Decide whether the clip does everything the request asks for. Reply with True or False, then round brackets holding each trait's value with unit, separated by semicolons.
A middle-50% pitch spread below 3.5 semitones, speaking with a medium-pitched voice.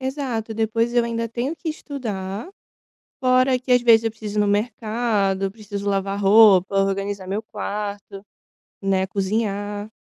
False (2.9 semitones; 210 Hz)